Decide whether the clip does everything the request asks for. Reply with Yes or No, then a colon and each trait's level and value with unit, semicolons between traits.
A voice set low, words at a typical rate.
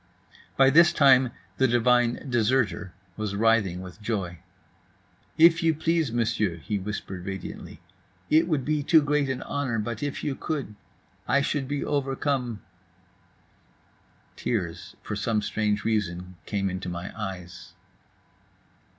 No: low, 115 Hz; slow, 125 wpm